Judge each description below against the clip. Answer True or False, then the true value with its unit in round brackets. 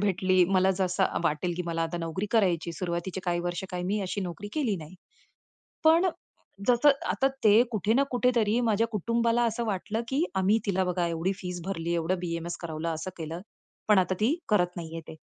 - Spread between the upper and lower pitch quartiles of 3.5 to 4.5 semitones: True (4.1 semitones)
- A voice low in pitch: False (185 Hz)